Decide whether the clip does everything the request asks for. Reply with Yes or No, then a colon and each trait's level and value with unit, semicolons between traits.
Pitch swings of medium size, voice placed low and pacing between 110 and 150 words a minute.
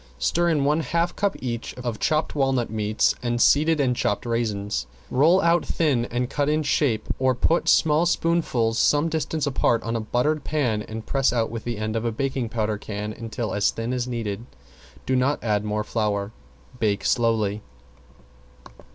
No: average, 5.0 semitones; low, 120 Hz; average, 175 wpm